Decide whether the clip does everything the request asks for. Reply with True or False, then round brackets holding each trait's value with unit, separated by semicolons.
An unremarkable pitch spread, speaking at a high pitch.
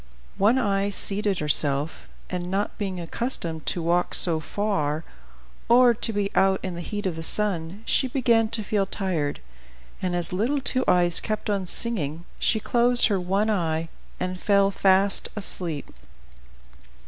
True (3.6 semitones; 195 Hz)